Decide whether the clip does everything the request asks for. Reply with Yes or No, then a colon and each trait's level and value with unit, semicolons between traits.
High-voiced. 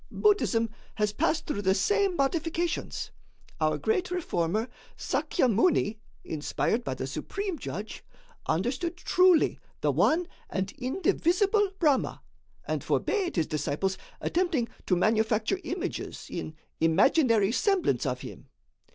Yes: very high, 255 Hz